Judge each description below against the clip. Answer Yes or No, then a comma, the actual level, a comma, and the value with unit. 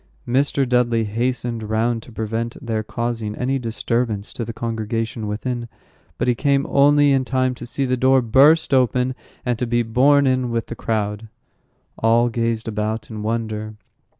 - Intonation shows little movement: Yes, narrow, 2.3 semitones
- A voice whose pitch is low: Yes, low, 120 Hz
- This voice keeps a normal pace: Yes, average, 165 wpm